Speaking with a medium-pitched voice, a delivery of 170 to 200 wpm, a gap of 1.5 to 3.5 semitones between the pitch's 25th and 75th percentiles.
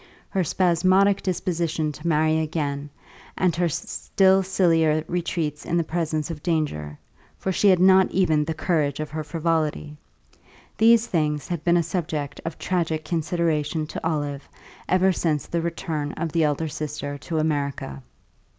No: medium, 160 Hz; average, 150 wpm; narrow, 2.6 semitones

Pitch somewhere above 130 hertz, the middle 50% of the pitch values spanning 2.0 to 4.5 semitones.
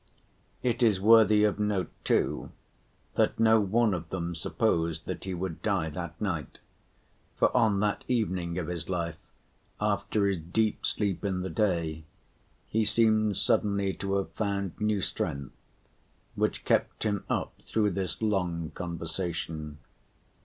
No: very low, 95 Hz; average, 4.0 semitones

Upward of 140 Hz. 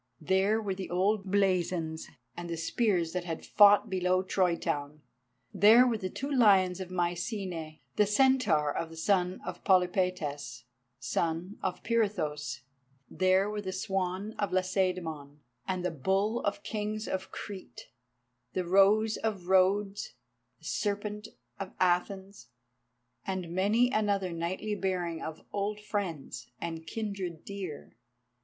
Yes: medium, 185 Hz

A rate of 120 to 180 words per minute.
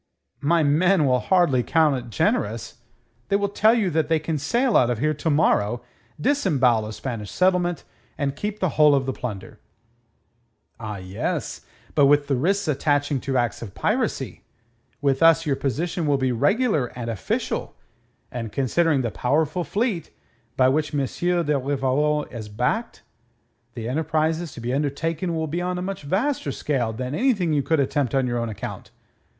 Yes: average, 170 wpm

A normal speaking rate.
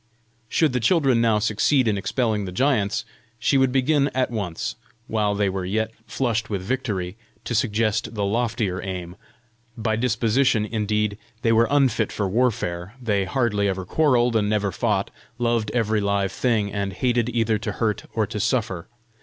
Yes: average, 165 wpm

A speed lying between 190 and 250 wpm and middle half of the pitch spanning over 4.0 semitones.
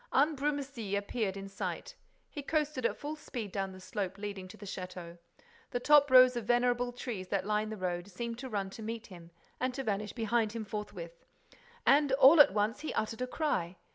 Yes: average, 200 wpm; average, 4.9 semitones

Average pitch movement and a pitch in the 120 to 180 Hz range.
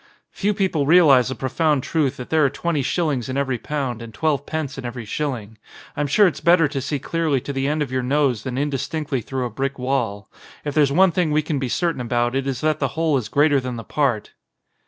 Yes: average, 3.3 semitones; medium, 140 Hz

